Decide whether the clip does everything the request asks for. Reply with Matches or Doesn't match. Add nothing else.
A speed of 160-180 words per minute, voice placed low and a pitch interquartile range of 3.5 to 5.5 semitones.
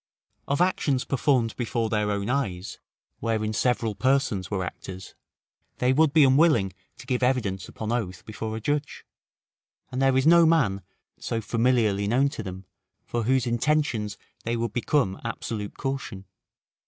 Doesn't match